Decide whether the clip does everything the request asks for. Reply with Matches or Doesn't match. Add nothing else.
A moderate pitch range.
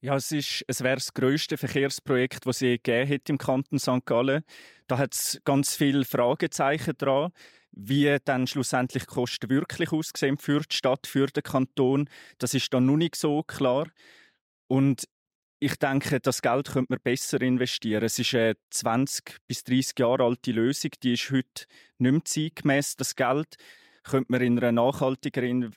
Doesn't match